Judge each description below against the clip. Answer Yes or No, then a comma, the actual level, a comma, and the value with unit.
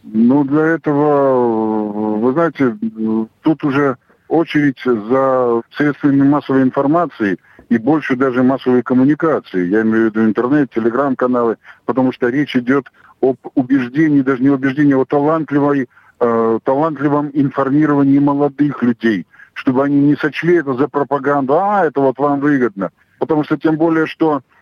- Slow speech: No, average, 135 wpm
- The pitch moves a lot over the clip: No, average, 2.8 semitones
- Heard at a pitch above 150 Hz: No, medium, 140 Hz